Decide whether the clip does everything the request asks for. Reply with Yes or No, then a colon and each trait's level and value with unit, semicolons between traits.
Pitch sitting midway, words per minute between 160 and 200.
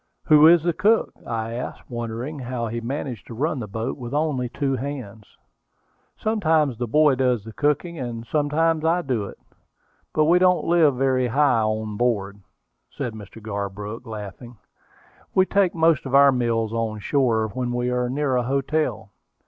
No: low, 125 Hz; average, 170 wpm